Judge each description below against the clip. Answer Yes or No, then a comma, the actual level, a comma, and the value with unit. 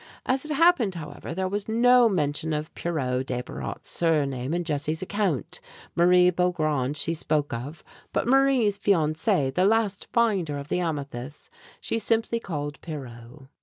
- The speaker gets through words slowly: No, average, 145 wpm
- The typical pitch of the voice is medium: Yes, medium, 165 Hz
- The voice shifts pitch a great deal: Yes, wide, 5.9 semitones